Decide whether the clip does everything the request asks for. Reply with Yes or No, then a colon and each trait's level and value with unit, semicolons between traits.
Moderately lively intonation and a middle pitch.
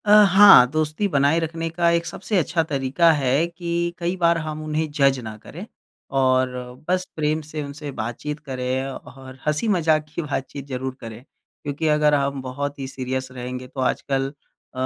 Yes: average, 3.9 semitones; medium, 145 Hz